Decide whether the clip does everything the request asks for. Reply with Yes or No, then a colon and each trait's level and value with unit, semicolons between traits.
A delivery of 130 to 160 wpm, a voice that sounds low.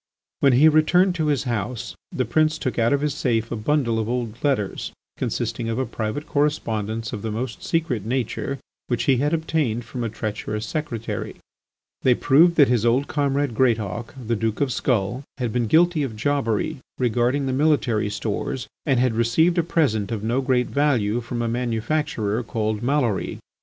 No: average, 180 wpm; low, 125 Hz